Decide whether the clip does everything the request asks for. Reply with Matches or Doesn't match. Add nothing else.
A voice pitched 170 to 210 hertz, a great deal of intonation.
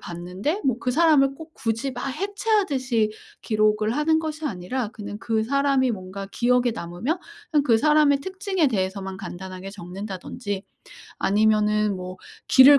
Doesn't match